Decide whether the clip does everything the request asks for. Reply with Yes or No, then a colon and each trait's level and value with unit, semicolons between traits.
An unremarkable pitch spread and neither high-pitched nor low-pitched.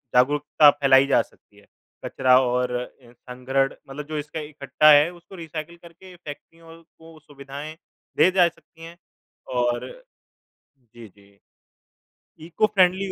Yes: average, 4.3 semitones; medium, 150 Hz